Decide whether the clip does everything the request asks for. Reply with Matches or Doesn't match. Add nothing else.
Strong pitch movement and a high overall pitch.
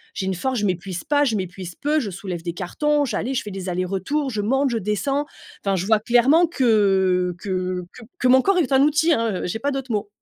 Matches